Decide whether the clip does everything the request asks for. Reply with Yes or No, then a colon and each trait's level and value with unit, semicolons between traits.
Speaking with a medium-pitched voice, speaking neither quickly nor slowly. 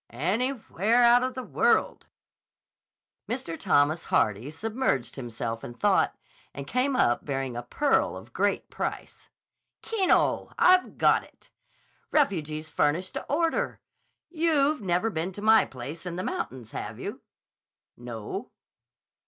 No: medium, 180 Hz; slow, 130 wpm